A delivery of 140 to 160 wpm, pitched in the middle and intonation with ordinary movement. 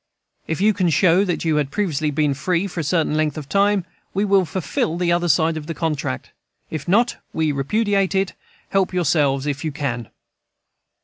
No: average, 190 wpm; medium, 165 Hz; average, 4.2 semitones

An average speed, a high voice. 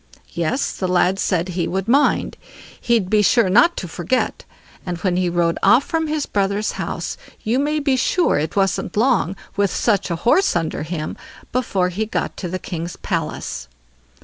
Yes: average, 175 wpm; high, 195 Hz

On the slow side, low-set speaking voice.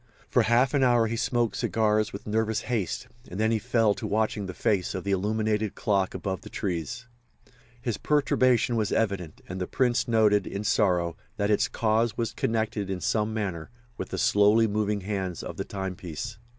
No: average, 185 wpm; low, 105 Hz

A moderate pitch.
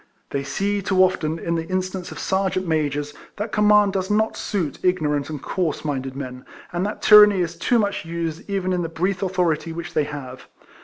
Yes: medium, 175 Hz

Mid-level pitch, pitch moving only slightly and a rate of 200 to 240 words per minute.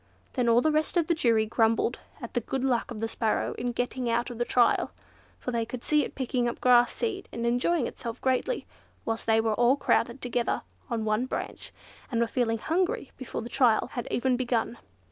No: high, 240 Hz; narrow, 2.1 semitones; fast, 205 wpm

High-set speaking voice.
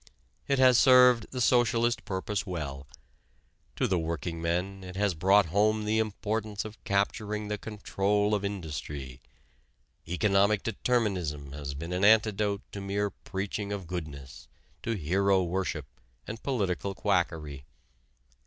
No: low, 100 Hz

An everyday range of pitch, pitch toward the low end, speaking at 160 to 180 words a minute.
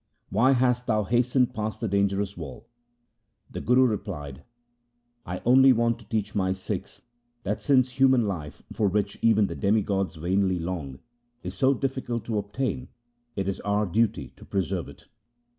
Yes: average, 4.0 semitones; low, 105 Hz; average, 165 wpm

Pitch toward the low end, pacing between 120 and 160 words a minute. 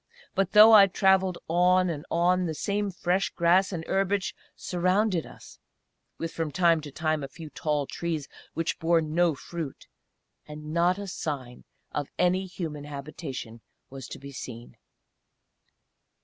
No: medium, 170 Hz; average, 150 wpm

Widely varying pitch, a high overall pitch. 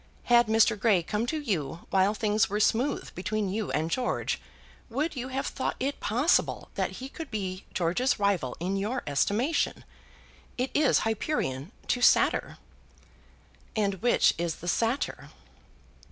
No: average, 5.0 semitones; high, 215 Hz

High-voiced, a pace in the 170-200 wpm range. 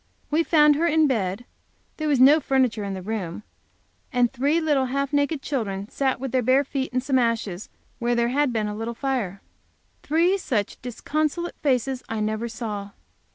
Yes: very high, 255 Hz; average, 180 wpm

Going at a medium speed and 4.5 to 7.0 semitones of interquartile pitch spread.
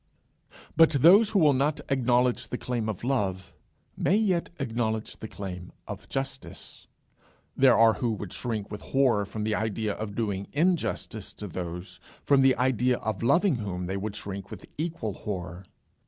Yes: average, 165 wpm; average, 5.0 semitones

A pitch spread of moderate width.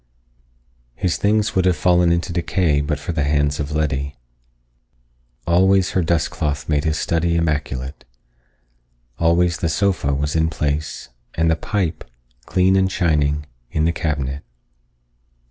Yes: average, 3.1 semitones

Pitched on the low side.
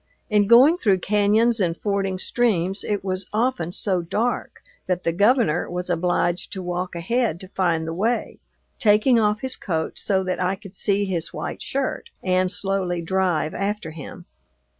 No: high, 190 Hz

